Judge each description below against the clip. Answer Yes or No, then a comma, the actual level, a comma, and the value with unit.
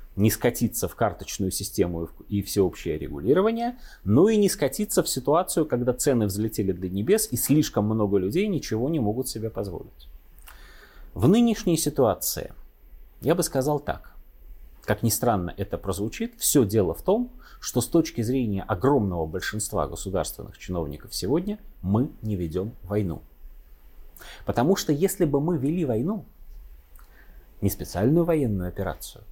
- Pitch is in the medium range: No, low, 105 Hz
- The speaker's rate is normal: Yes, average, 140 wpm